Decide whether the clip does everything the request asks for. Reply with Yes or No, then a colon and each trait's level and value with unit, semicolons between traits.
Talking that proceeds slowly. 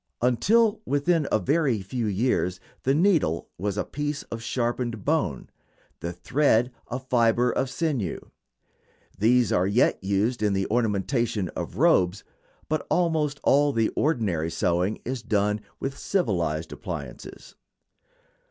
Yes: slow, 130 wpm